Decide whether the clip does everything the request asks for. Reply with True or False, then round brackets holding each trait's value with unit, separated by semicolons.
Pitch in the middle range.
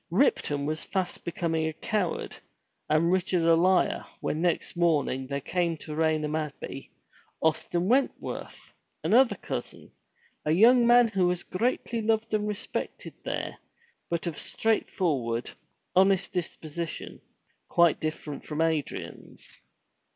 True (170 Hz)